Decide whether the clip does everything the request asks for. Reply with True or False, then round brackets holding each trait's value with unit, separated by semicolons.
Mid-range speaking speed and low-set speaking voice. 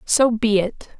False (180 wpm; 220 Hz)